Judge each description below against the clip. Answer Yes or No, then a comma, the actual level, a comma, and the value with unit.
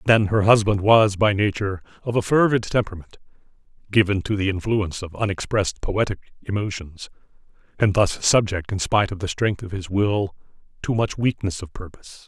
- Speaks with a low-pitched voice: Yes, low, 100 Hz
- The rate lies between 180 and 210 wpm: No, average, 165 wpm